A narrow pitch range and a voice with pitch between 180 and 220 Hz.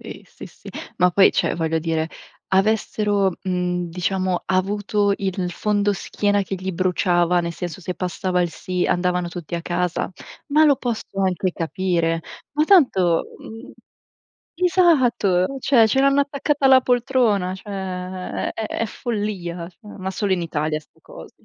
No: average, 3.5 semitones; high, 190 Hz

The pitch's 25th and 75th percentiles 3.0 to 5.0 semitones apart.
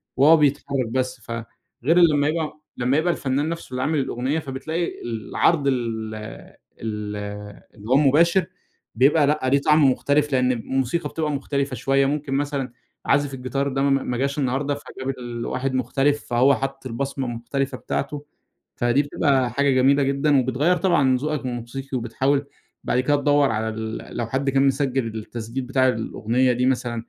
No: narrow, 2.4 semitones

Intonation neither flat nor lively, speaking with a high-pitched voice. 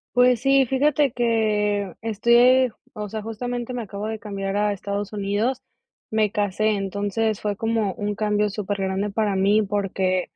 No: narrow, 2.1 semitones; high, 210 Hz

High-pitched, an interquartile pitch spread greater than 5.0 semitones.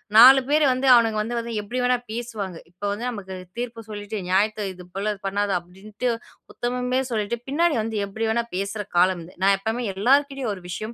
No: high, 215 Hz; average, 3.8 semitones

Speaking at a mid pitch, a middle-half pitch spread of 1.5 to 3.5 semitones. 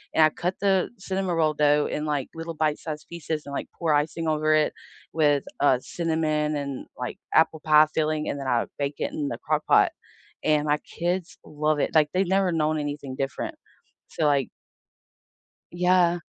Yes: medium, 155 Hz; narrow, 2.4 semitones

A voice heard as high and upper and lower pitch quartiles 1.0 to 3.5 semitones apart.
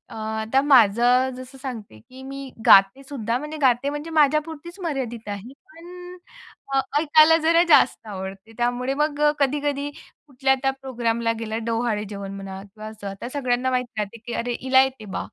No: very high, 255 Hz; average, 4.3 semitones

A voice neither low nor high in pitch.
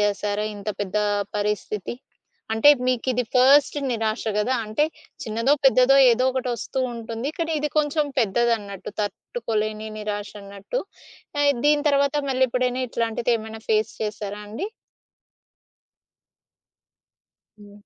No: high, 230 Hz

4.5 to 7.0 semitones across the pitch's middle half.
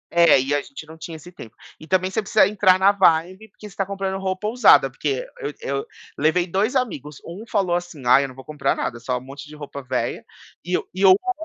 Yes: average, 5.0 semitones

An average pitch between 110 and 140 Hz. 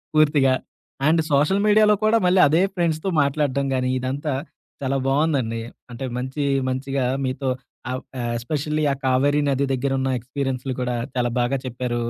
Yes: low, 135 Hz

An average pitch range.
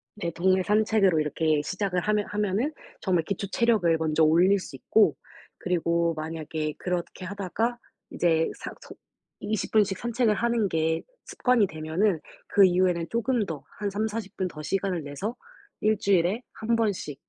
Yes: average, 4.5 semitones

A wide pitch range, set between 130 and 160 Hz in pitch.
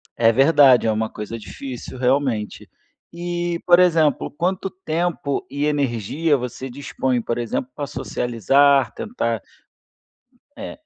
Yes: wide, 5.7 semitones; medium, 140 Hz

